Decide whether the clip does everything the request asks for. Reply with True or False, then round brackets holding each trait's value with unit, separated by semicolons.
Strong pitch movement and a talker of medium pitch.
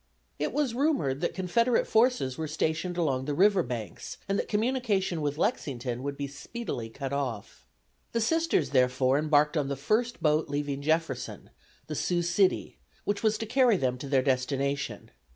True (7.3 semitones; 155 Hz)